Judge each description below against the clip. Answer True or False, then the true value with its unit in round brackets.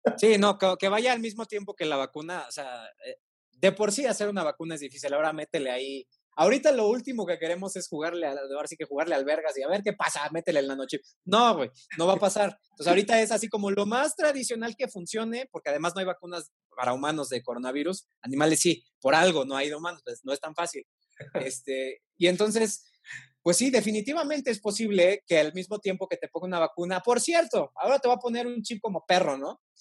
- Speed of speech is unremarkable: False (225 wpm)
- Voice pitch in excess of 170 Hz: True (190 Hz)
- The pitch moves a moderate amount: False (6.3 semitones)